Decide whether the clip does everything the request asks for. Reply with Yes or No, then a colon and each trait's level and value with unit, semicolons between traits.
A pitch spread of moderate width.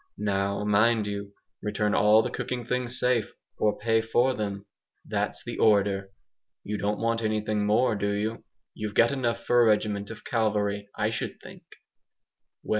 No: narrow, 2.2 semitones